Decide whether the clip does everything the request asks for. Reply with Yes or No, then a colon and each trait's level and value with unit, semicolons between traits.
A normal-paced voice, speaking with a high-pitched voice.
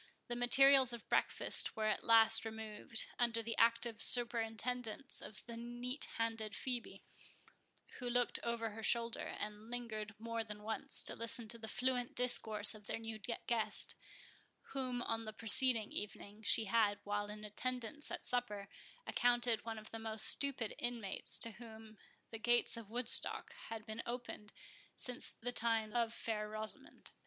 Yes: average, 155 wpm; high, 230 Hz